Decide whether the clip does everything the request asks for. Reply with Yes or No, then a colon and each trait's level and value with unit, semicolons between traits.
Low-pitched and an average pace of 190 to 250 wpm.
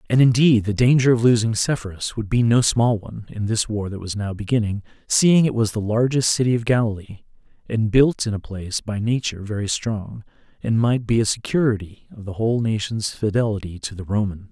Yes: low, 110 Hz; average, 200 wpm